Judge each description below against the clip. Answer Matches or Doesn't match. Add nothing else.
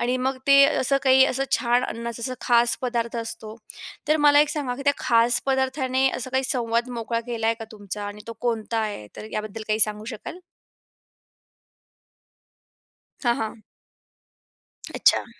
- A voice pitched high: Matches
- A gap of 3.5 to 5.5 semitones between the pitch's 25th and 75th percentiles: Doesn't match